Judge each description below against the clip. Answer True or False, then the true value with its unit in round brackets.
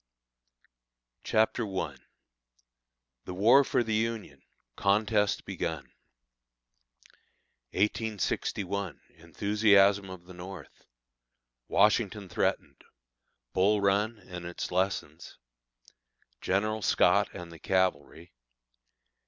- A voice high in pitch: False (100 Hz)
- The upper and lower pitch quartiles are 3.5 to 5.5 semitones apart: False (2.7 semitones)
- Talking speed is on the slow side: True (80 wpm)